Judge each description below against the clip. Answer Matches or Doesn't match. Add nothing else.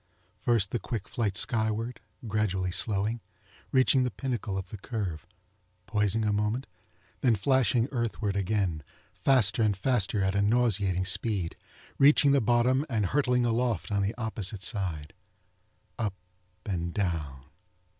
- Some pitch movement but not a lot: Matches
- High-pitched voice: Doesn't match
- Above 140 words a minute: Doesn't match